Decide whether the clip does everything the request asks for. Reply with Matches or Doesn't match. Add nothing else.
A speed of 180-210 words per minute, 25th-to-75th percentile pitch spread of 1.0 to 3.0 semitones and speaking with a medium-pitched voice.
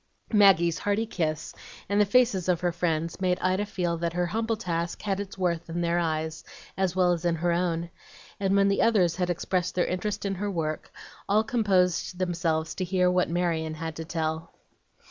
Matches